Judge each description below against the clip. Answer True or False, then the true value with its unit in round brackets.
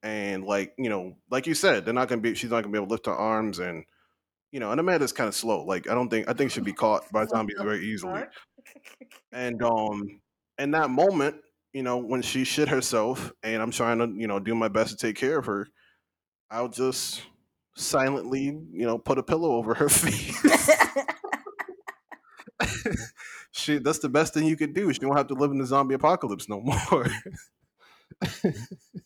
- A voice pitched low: True (130 Hz)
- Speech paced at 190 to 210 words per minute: True (200 wpm)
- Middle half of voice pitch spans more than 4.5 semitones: True (5.3 semitones)